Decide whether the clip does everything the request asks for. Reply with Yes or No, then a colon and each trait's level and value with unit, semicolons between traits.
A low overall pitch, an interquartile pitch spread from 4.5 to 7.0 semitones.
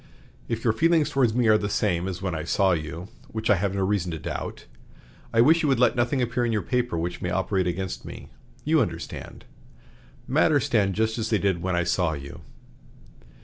Yes: low, 100 Hz; average, 5.1 semitones